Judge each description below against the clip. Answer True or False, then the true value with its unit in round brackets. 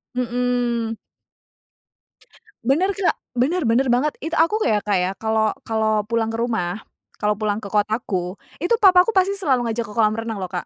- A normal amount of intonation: True (4.2 semitones)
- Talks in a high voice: True (230 Hz)